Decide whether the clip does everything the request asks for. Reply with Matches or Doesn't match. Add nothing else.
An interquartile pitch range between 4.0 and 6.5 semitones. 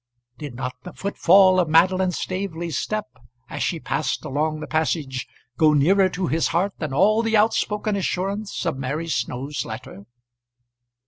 Matches